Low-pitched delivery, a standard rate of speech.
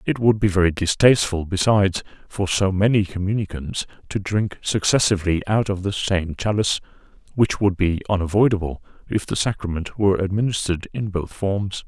Yes: low, 100 Hz; average, 150 wpm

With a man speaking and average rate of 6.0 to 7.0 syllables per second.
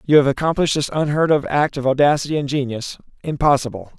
Yes: male; 6.6 syllables/s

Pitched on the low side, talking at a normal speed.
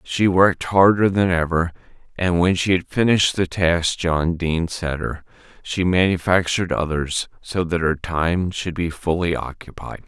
Yes: very low, 85 Hz; average, 160 wpm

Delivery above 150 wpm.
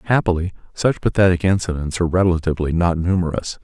No: slow, 130 wpm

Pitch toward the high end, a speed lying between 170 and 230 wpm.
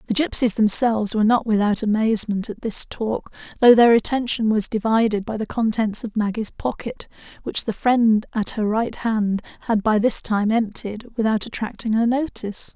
Yes: high, 220 Hz; average, 175 wpm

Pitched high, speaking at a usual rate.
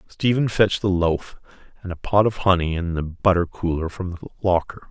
No: very low, 90 Hz; average, 185 wpm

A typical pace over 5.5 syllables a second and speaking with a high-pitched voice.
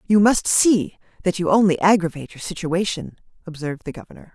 No: 5.9 syllables/s; medium, 180 Hz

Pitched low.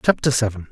Yes: low, 120 Hz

